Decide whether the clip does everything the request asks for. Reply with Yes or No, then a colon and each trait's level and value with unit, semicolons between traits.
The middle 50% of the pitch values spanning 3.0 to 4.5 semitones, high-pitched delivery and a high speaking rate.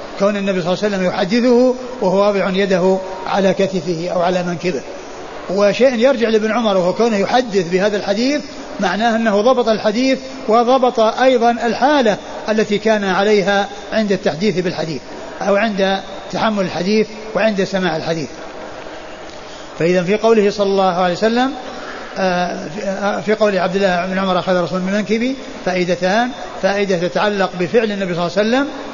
Yes: average, 3.6 semitones; high, 200 Hz; fast, 145 wpm